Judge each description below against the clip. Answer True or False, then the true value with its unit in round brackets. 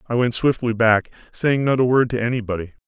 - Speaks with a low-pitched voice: True (120 Hz)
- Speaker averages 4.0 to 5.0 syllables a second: False (5.7 syllables/s)